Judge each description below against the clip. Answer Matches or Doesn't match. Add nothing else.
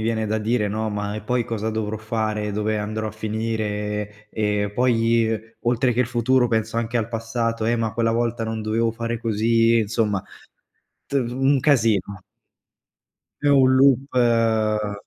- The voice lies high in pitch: Doesn't match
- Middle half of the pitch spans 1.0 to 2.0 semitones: Matches